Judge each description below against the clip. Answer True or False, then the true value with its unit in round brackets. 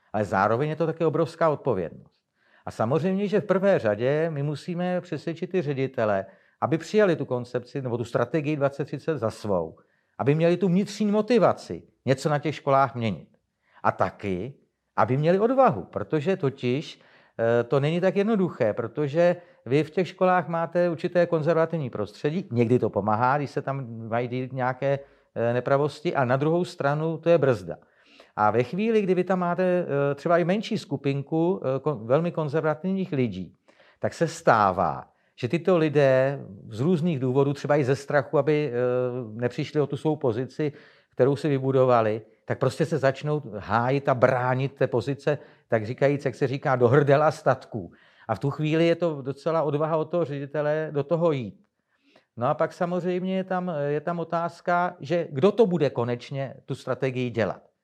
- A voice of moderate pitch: True (145 Hz)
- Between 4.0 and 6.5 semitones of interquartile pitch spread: True (4.9 semitones)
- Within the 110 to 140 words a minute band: False (165 wpm)